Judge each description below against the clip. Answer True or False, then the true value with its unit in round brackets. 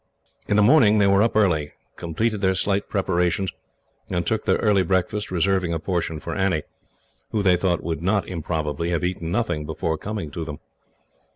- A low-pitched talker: True (95 Hz)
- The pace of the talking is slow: False (180 wpm)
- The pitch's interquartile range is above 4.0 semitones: False (3.6 semitones)